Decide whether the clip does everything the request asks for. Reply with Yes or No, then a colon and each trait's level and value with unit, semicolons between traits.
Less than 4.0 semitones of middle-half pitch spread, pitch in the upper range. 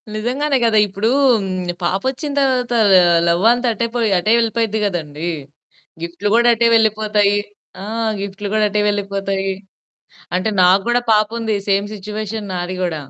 Yes: average, 2.8 semitones; high, 210 Hz